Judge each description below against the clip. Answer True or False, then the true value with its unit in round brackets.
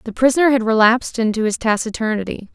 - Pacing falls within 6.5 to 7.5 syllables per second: True (6.6 syllables/s)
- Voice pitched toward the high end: True (230 Hz)